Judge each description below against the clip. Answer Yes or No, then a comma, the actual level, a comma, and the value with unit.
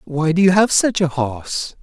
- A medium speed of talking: No, fast, 230 wpm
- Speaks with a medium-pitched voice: Yes, medium, 170 Hz